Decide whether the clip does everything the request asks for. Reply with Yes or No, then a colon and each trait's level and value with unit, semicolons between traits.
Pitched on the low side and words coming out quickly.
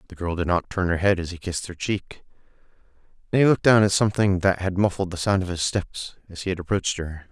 Yes: very low, 95 Hz; fast, 255 wpm